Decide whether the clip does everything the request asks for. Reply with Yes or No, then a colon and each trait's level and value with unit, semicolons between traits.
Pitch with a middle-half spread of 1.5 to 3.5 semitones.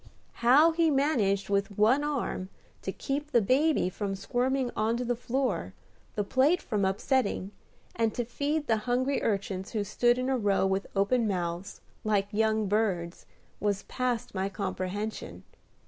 No: average, 4.7 semitones